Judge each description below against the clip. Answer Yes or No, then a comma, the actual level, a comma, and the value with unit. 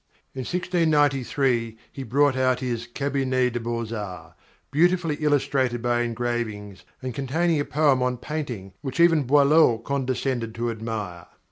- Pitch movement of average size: Yes, average, 3.6 semitones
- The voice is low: Yes, low, 130 Hz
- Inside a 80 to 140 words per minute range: Yes, slow, 135 wpm